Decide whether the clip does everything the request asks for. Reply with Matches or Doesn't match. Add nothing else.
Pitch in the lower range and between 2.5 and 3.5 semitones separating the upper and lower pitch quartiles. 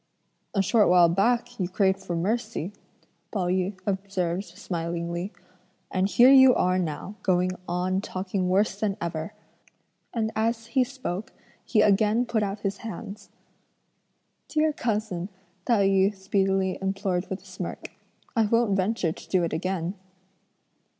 Doesn't match